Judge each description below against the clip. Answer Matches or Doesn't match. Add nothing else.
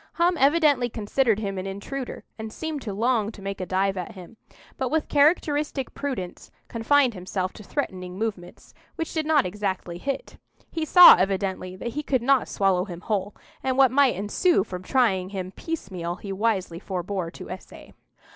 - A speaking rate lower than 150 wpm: Doesn't match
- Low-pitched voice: Doesn't match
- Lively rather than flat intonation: Matches